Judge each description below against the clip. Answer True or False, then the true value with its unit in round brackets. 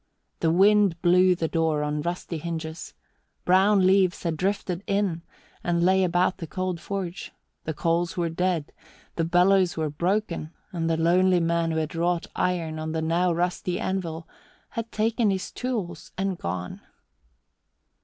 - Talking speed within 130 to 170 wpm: True (155 wpm)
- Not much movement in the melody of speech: True (2.3 semitones)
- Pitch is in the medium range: True (175 Hz)